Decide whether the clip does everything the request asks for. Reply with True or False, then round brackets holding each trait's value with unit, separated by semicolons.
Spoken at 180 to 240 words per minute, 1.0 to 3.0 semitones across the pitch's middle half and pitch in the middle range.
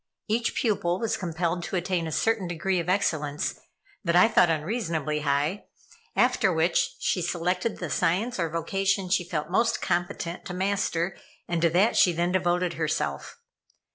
False (160 wpm; 2.6 semitones; 175 Hz)